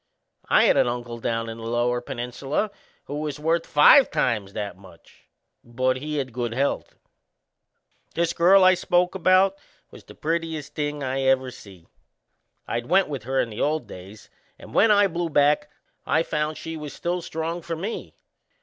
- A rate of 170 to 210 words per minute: Yes, average, 175 wpm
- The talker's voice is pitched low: No, medium, 145 Hz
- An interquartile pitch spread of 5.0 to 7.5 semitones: Yes, wide, 5.6 semitones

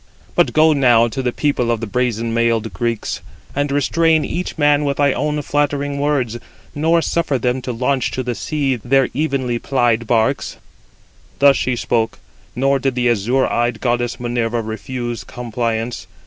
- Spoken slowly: No, average, 165 wpm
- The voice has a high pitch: No, low, 125 Hz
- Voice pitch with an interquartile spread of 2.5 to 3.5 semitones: Yes, average, 3.2 semitones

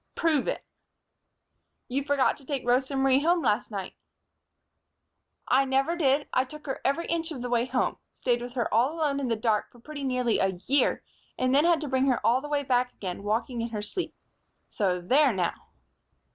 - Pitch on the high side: Yes, very high, 260 Hz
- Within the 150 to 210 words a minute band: Yes, average, 200 wpm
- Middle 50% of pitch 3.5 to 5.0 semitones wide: No, average, 3.0 semitones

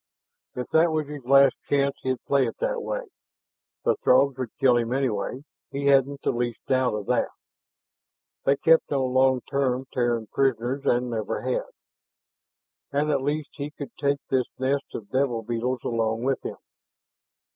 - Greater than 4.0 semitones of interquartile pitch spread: No, narrow, 2.4 semitones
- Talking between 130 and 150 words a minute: No, average, 165 wpm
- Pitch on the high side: No, low, 130 Hz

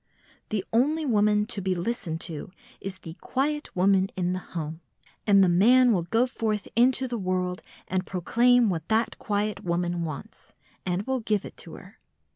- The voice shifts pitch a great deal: No, average, 4.7 semitones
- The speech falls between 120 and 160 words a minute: No, average, 170 wpm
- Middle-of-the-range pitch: No, high, 200 Hz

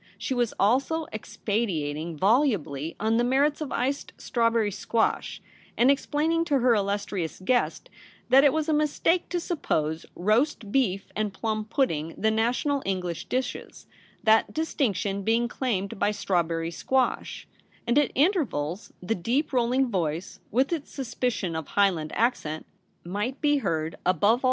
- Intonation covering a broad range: Yes, wide, 6.2 semitones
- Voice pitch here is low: No, high, 225 Hz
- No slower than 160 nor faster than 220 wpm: No, average, 150 wpm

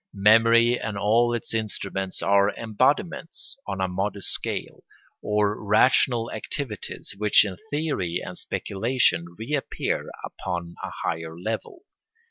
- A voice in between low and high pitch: No, low, 105 Hz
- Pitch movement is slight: No, average, 3.6 semitones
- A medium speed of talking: No, slow, 115 wpm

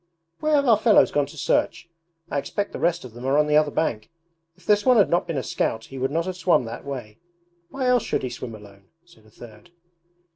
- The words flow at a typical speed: No, fast, 245 wpm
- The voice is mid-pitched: Yes, medium, 145 Hz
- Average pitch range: No, wide, 7.6 semitones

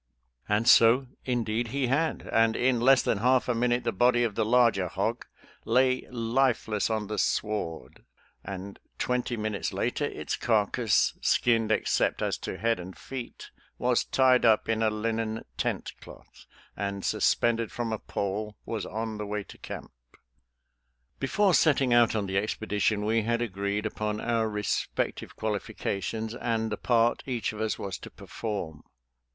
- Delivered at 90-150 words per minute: No, average, 160 wpm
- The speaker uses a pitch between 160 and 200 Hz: No, low, 110 Hz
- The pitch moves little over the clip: Yes, narrow, 2.3 semitones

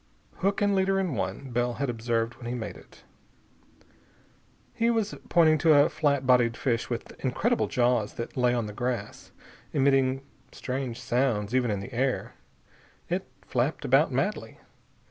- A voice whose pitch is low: Yes, low, 125 Hz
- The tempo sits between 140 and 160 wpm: Yes, average, 155 wpm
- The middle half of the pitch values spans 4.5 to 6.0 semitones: No, average, 3.4 semitones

